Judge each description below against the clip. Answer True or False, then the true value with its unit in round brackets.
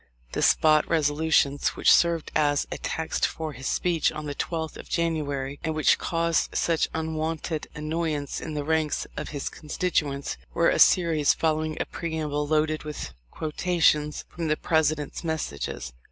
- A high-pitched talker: False (155 Hz)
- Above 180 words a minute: False (155 wpm)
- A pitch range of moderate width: False (1.6 semitones)